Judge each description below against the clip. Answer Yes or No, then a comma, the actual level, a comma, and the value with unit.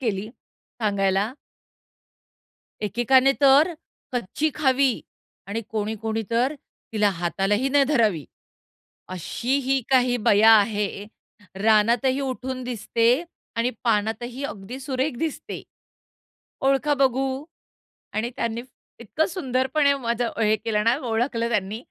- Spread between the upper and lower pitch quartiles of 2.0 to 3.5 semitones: No, average, 3.9 semitones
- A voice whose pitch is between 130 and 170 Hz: No, high, 235 Hz